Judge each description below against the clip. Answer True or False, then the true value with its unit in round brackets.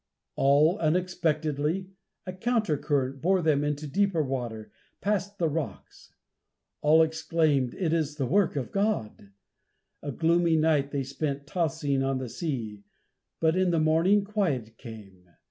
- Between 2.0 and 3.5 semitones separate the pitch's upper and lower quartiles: False (4.2 semitones)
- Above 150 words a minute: False (140 wpm)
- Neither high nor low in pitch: True (155 Hz)